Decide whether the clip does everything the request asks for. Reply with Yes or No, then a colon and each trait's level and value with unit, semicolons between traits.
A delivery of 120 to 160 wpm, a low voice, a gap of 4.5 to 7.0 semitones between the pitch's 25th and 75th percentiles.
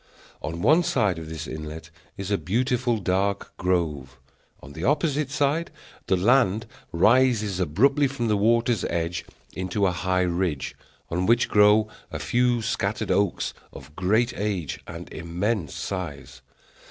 Yes: average, 140 wpm; low, 100 Hz; wide, 5.5 semitones